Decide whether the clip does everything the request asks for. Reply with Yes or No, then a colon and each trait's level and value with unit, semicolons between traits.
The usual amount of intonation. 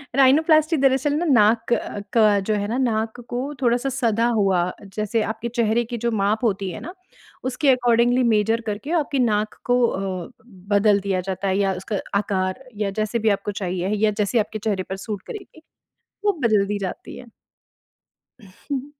Yes: average, 3.7 semitones